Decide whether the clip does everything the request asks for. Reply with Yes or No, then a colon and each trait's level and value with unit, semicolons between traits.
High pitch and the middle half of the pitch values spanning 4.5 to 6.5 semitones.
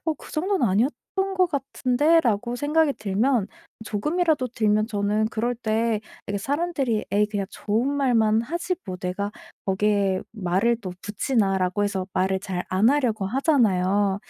Yes: high, 220 Hz; wide, 5.5 semitones